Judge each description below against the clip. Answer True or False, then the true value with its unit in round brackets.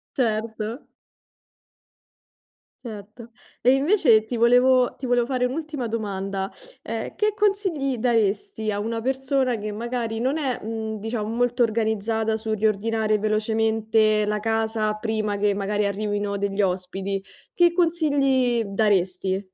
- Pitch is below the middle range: False (220 Hz)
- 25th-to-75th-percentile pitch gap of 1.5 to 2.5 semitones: False (2.9 semitones)